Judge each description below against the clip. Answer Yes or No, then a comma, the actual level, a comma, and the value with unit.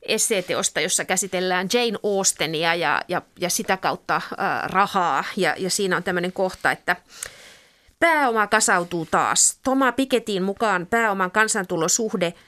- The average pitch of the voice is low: No, high, 195 Hz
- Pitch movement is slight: No, average, 3.8 semitones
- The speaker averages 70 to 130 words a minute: Yes, average, 125 wpm